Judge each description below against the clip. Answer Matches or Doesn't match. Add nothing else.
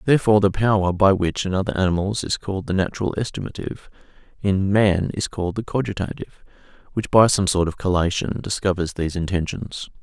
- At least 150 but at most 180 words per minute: Matches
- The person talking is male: Matches